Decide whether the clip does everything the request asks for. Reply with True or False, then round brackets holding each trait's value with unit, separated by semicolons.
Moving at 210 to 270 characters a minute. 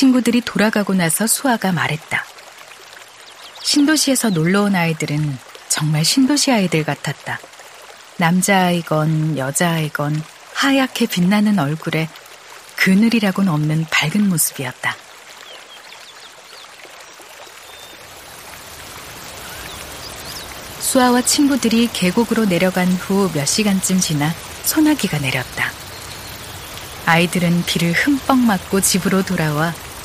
True (235 characters per minute)